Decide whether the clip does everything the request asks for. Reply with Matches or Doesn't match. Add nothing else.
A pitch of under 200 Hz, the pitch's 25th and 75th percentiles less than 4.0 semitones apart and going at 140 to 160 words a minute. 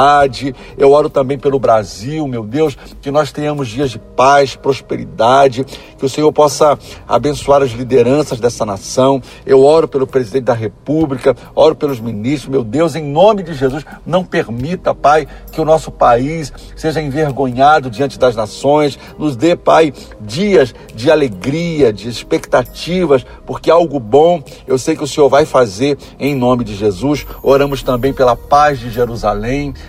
Matches